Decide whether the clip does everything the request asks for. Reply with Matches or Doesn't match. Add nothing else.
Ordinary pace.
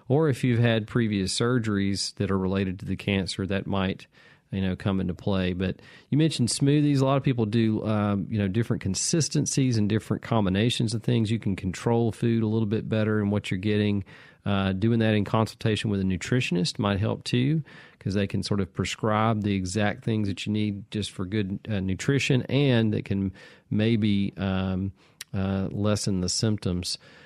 Matches